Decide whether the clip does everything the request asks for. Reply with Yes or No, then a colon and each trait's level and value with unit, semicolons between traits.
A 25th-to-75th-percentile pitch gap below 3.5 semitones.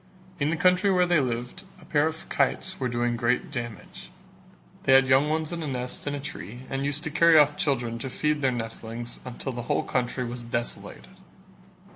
No: average, 4.0 semitones